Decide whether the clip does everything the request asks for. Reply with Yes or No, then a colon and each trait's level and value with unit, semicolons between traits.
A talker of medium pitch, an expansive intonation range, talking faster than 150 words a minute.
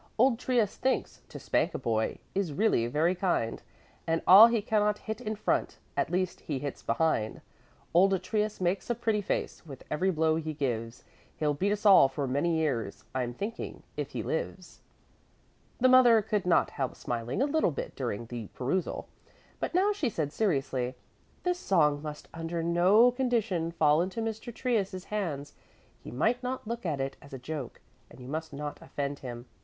Yes: medium, 170 Hz; wide, 7.4 semitones; average, 180 wpm